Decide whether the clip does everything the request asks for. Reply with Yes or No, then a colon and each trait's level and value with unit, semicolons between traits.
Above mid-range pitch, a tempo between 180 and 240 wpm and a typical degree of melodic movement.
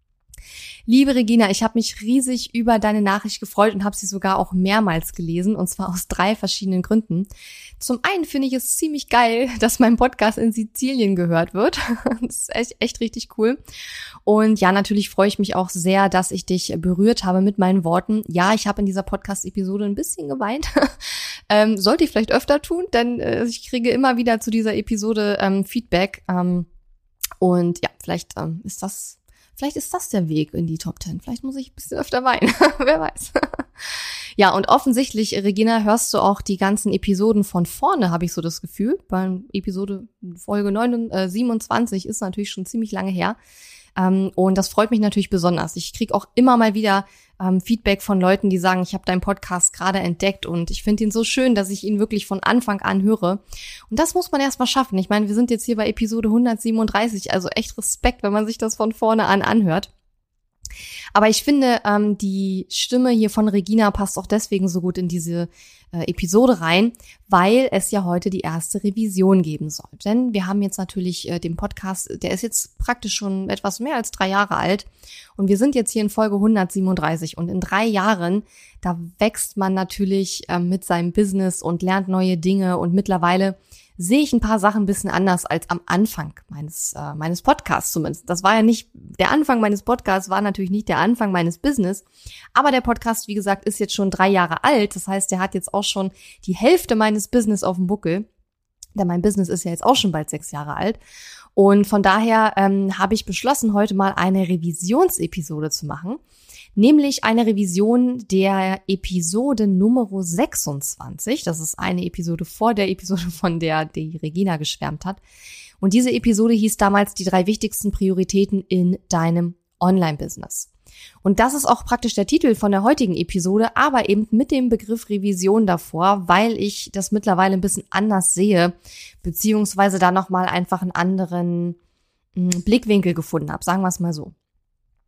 Yes: high, 200 Hz; fast, 190 wpm; average, 3.3 semitones